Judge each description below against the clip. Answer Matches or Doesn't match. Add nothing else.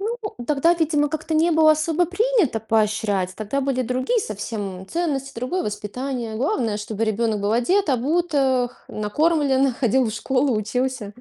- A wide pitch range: Matches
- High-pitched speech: Matches